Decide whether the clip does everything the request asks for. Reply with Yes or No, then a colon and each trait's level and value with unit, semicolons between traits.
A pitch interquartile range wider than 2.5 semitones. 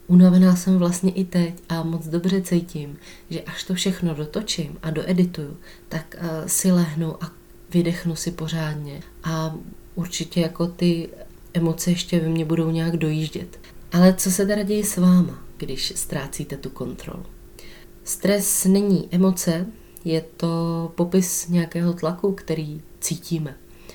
No: narrow, 2.0 semitones